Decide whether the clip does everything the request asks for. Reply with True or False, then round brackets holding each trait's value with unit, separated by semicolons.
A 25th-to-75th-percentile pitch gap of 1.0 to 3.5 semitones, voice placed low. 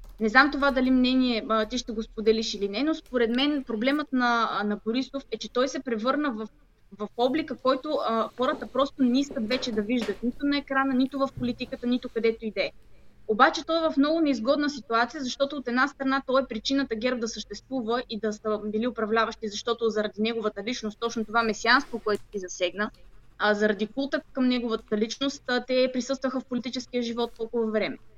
False (3.2 semitones; 245 Hz)